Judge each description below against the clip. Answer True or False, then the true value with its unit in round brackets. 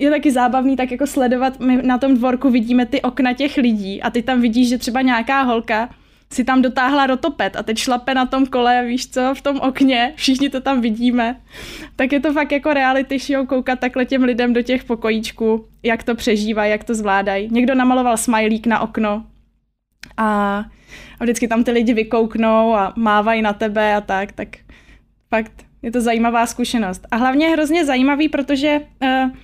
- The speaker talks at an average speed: False (190 wpm)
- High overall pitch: True (250 Hz)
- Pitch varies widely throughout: False (2.7 semitones)